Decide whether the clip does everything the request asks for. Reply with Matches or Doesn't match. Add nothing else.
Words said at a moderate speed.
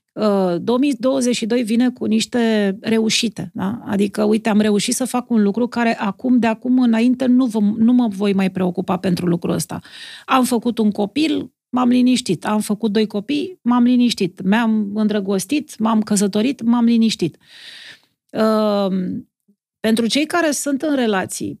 Matches